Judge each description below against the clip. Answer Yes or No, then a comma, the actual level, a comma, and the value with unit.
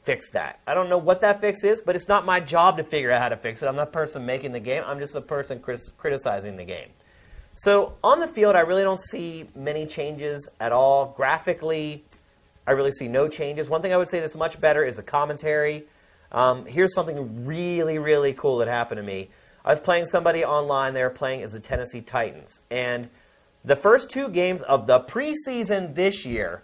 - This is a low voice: No, medium, 150 Hz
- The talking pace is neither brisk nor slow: No, fast, 215 wpm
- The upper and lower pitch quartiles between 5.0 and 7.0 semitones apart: Yes, average, 5.3 semitones